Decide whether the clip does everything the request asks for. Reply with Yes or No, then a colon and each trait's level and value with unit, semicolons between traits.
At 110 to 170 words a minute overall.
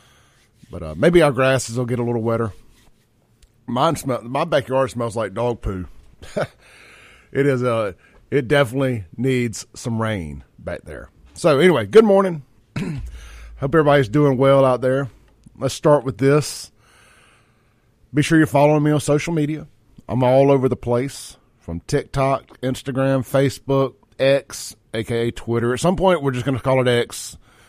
Yes: average, 155 wpm